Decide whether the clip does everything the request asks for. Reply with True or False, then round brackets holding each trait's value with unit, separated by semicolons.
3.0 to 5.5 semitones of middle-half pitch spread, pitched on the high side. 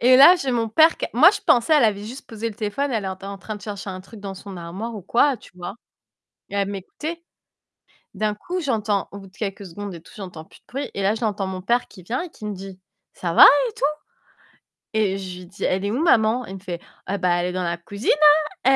True (3.7 semitones; 205 Hz)